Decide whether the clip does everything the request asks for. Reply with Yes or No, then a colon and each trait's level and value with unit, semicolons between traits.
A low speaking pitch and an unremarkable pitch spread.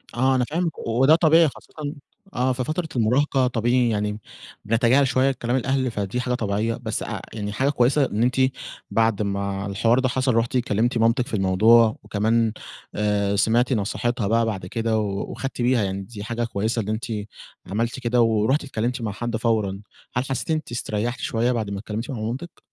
Yes: low, 115 Hz; average, 3.0 semitones